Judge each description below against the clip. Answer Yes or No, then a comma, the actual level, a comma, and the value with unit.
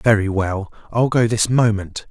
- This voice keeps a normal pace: Yes, average, 170 wpm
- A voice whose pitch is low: Yes, low, 110 Hz